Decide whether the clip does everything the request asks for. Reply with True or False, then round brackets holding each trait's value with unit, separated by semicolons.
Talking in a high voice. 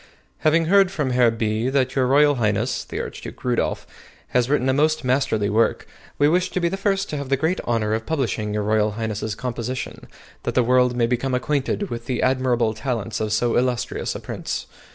False (125 Hz)